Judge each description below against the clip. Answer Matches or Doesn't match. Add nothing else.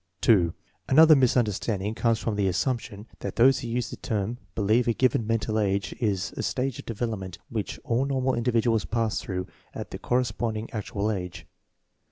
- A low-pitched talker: Matches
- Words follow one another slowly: Doesn't match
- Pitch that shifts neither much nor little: Matches